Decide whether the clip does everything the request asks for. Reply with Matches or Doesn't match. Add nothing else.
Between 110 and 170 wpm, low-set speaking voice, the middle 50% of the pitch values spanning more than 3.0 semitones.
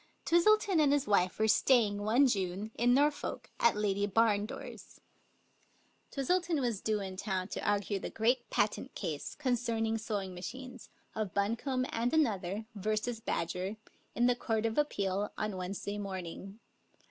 Doesn't match